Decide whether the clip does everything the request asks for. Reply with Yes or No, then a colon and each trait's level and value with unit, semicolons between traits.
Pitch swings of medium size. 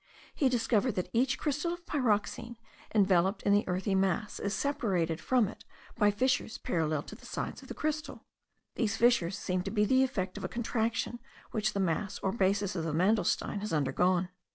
Yes: average, 4.4 semitones